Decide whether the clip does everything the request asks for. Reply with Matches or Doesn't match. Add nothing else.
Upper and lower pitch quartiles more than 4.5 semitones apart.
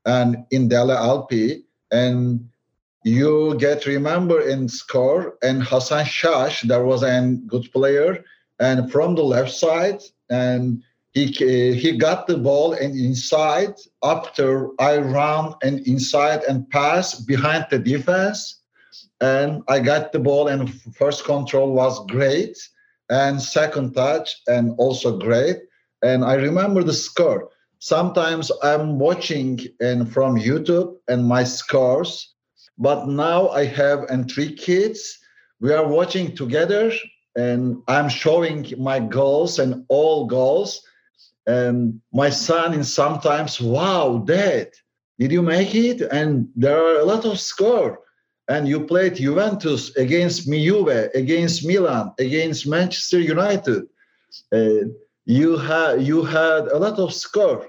Matches